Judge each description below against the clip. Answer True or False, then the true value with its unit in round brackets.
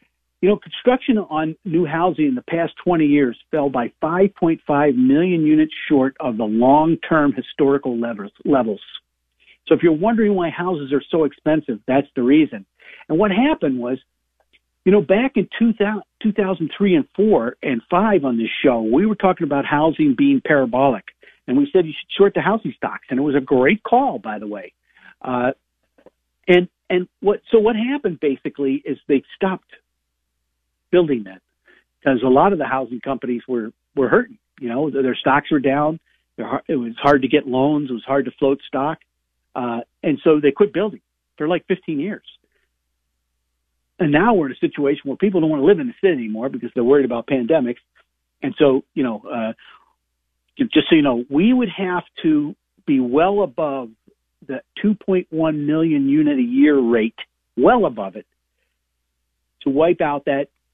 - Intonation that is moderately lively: False (7.8 semitones)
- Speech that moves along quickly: False (185 wpm)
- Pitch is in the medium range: True (155 Hz)